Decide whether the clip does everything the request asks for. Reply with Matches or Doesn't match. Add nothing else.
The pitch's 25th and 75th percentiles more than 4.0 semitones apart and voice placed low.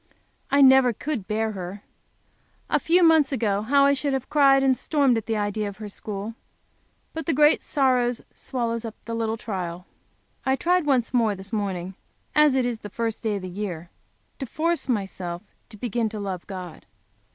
Doesn't match